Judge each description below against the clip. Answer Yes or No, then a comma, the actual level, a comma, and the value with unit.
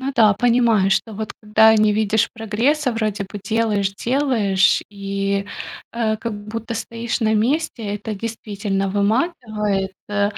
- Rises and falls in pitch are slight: Yes, narrow, 2.3 semitones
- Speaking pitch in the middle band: No, high, 215 Hz